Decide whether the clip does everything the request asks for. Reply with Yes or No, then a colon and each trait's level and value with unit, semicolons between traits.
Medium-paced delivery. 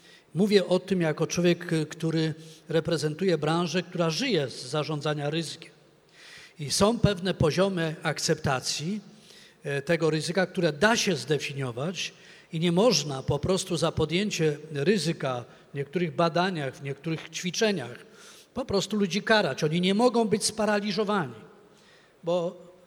Yes: average, 125 wpm